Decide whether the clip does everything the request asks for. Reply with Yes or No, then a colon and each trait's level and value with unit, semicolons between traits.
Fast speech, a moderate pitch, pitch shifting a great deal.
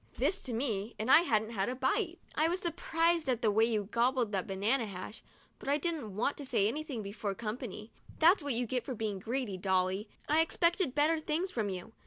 No: fast, 215 wpm; high, 240 Hz; wide, 6.4 semitones